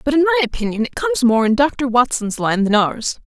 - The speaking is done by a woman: Yes, female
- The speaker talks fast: Yes, fast, 240 wpm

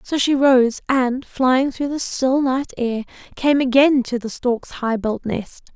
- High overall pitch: Yes, very high, 255 Hz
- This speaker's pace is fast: No, average, 190 wpm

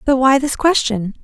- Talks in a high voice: Yes, very high, 260 Hz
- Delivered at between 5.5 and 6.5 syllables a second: No, 4.6 syllables/s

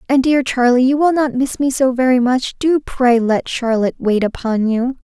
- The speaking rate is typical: No, fast, 215 wpm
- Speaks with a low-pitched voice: No, very high, 255 Hz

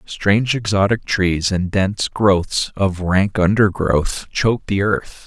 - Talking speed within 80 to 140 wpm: Yes, slow, 135 wpm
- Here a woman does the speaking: No, male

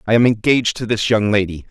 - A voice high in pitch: No, low, 110 Hz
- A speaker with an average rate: No, fast, 245 wpm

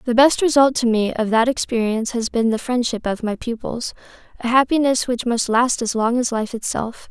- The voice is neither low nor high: No, high, 240 Hz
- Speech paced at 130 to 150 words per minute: No, fast, 205 wpm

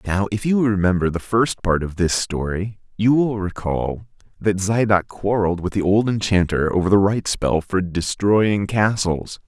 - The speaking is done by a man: Yes, male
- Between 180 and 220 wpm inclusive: No, average, 170 wpm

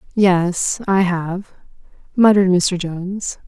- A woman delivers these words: Yes, female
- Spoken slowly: Yes, slow, 105 wpm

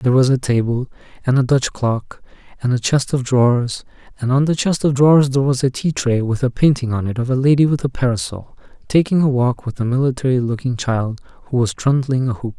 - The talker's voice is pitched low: Yes, low, 130 Hz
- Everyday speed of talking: No, fast, 230 wpm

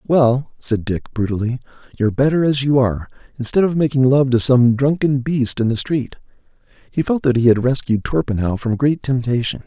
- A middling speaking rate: Yes, average, 185 wpm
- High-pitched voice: No, low, 130 Hz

